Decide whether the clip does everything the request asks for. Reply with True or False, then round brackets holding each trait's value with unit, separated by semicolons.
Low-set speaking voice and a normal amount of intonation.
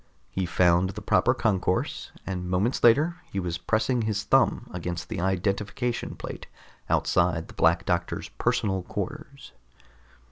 True (95 Hz; 4.3 semitones)